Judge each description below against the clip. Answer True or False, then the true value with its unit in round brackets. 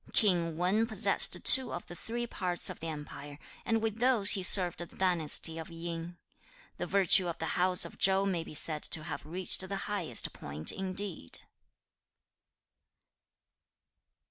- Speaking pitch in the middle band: True (180 Hz)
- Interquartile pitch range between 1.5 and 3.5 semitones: True (3.2 semitones)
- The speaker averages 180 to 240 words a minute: False (155 wpm)